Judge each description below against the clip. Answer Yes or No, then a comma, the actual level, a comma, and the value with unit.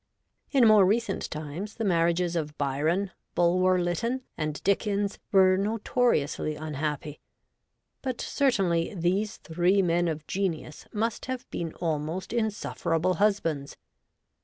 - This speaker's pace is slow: Yes, slow, 120 wpm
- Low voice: No, medium, 180 Hz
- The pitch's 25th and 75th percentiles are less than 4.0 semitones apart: No, average, 4.4 semitones